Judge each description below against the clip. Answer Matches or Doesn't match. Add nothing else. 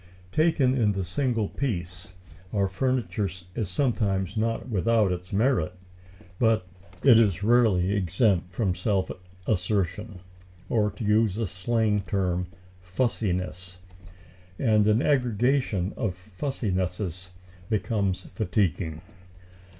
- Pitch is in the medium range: Doesn't match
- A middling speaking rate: Doesn't match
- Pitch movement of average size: Matches